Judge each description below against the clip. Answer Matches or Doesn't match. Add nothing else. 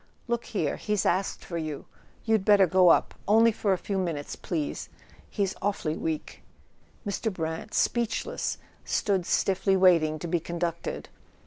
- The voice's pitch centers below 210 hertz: Matches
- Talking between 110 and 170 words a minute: Matches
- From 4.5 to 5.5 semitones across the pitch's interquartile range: Doesn't match